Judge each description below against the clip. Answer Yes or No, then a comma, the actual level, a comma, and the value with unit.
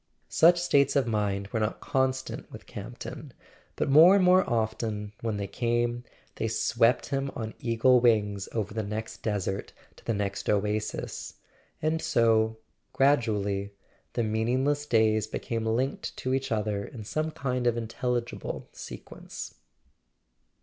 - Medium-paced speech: Yes, average, 145 wpm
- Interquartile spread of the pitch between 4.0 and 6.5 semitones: No, average, 3.6 semitones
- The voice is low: Yes, low, 115 Hz